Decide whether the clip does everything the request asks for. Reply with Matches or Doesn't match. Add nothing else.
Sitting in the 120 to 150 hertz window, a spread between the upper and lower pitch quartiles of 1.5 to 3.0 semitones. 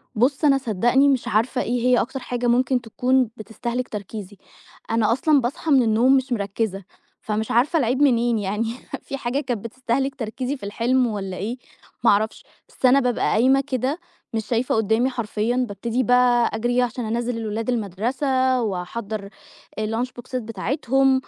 Doesn't match